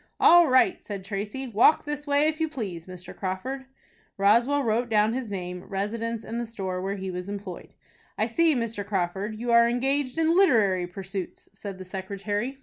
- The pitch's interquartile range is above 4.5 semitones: Yes, average, 5.1 semitones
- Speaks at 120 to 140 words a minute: No, average, 180 wpm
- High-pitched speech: Yes, high, 215 Hz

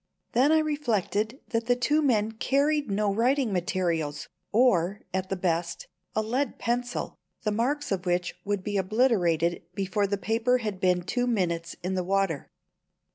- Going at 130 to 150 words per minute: No, average, 160 wpm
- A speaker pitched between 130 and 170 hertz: No, high, 210 Hz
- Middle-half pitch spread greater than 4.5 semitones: Yes, average, 5.2 semitones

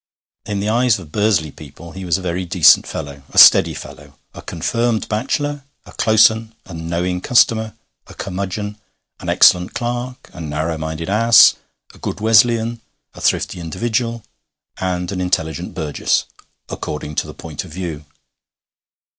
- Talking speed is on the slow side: No, average, 155 wpm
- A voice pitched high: No, very low, 95 Hz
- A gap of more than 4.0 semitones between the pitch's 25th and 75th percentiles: Yes, wide, 5.4 semitones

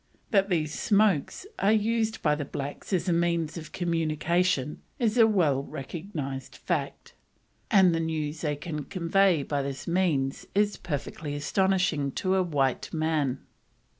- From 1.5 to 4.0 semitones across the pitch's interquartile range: No, average, 4.6 semitones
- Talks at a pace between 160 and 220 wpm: No, average, 145 wpm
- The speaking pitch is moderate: Yes, medium, 165 Hz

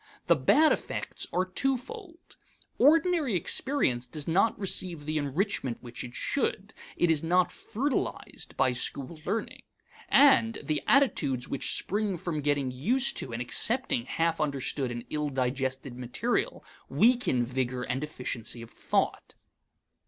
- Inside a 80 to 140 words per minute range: Yes, slow, 135 wpm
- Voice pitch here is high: No, medium, 155 Hz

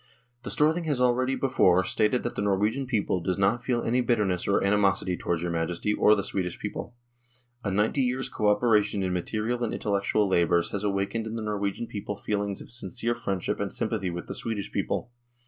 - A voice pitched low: Yes, low, 105 Hz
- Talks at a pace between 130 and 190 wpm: No, average, 200 wpm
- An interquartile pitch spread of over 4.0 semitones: No, average, 3.7 semitones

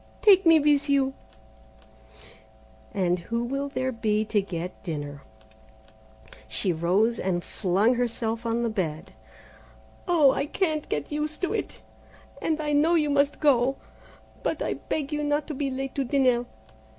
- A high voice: Yes, very high, 255 Hz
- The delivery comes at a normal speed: Yes, average, 150 wpm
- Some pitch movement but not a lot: No, wide, 6.4 semitones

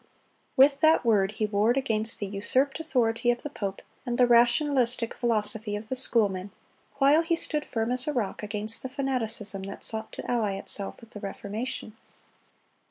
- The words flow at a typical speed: Yes, average, 170 wpm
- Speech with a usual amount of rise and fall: Yes, average, 3.7 semitones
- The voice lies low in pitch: No, high, 230 Hz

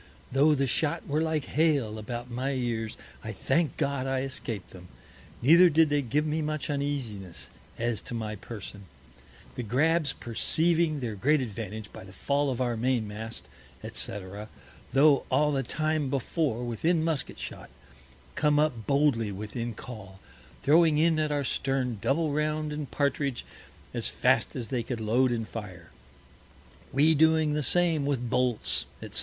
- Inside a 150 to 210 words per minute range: Yes, average, 160 wpm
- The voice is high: No, low, 135 Hz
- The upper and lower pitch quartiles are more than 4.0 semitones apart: Yes, average, 4.8 semitones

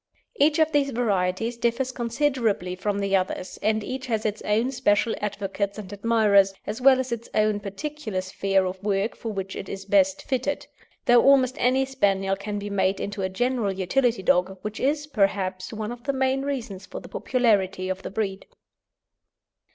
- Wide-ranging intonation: No, average, 4.7 semitones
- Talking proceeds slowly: No, average, 180 wpm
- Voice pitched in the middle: No, high, 215 Hz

